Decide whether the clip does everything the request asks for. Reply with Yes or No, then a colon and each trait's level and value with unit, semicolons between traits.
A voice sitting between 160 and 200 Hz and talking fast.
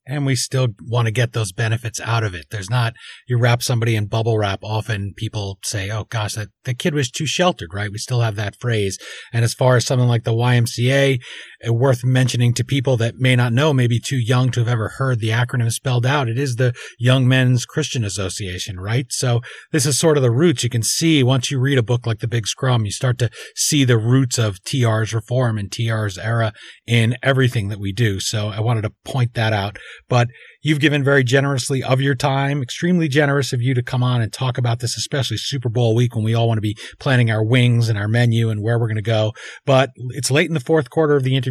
No: low, 120 Hz; fast, 240 wpm